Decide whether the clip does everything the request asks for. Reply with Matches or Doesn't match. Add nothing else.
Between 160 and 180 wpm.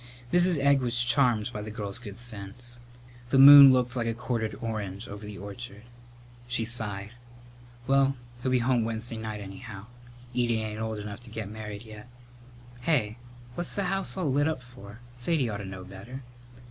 Matches